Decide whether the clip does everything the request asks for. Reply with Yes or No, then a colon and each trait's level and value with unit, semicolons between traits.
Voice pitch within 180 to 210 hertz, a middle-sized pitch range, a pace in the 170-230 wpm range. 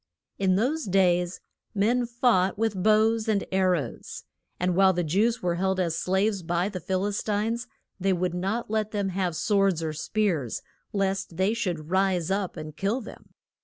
Yes: high, 190 Hz; average, 3.1 semitones; average, 175 wpm